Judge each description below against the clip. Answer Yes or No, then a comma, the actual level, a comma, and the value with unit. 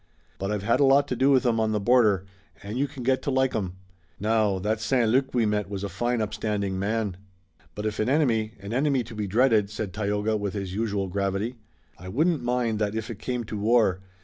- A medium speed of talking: No, fast, 230 wpm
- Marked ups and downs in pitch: No, average, 3.3 semitones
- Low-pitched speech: Yes, low, 110 Hz